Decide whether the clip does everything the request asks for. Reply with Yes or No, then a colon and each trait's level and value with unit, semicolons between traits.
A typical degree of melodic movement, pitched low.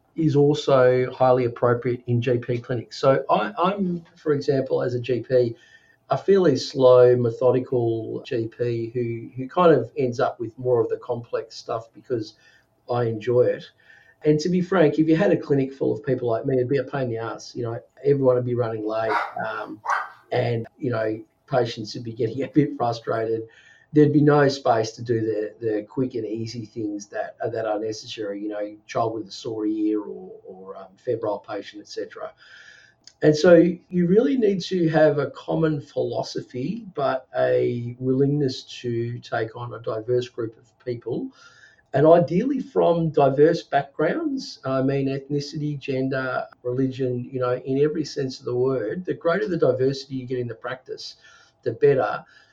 Yes: average, 4.2 semitones; low, 130 Hz